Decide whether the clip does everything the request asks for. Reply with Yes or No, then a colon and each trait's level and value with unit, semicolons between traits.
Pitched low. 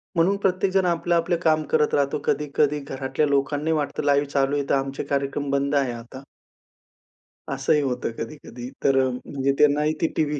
No: medium, 145 Hz